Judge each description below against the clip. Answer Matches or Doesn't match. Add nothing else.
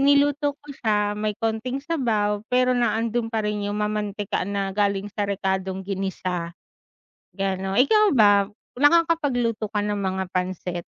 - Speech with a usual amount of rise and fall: Matches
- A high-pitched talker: Matches